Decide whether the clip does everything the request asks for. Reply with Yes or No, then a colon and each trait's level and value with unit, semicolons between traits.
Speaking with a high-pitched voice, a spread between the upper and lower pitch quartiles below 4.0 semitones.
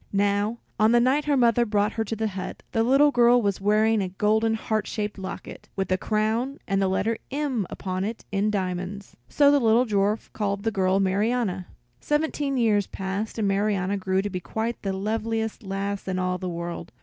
Yes: high, 210 Hz; average, 2.8 semitones